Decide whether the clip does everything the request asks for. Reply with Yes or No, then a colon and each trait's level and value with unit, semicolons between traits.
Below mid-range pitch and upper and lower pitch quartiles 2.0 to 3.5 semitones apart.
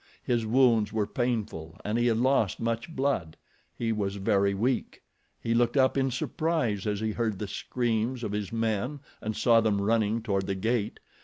Yes: low, 115 Hz; average, 2.9 semitones